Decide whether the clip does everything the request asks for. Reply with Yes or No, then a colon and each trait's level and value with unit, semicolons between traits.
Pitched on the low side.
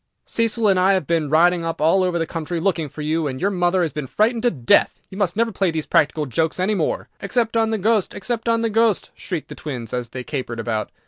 No: medium, 175 Hz